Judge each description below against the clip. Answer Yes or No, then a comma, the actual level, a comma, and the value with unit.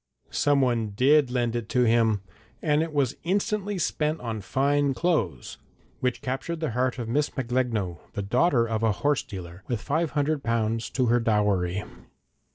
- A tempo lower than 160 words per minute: No, average, 165 wpm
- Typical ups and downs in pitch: Yes, average, 4.6 semitones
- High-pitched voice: No, low, 125 Hz